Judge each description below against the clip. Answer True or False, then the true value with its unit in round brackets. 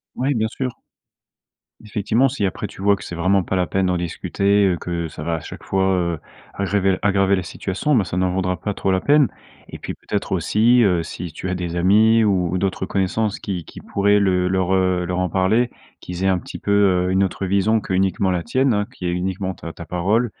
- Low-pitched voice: True (95 Hz)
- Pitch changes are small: True (2.2 semitones)